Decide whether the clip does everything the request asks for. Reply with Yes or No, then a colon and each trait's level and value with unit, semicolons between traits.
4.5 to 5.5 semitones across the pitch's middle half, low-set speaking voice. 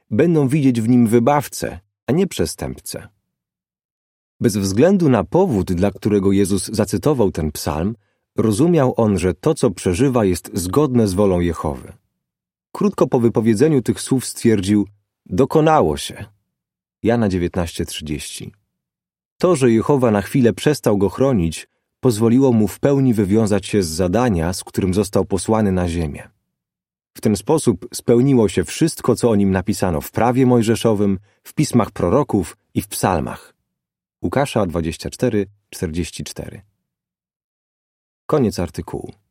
Yes: average, 5.0 semitones; low, 105 Hz